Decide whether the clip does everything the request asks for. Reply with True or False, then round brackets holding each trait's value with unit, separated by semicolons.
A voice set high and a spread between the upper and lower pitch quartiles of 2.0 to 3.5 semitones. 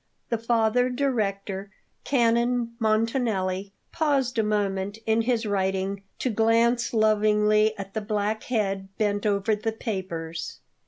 True (215 Hz; 2.7 semitones)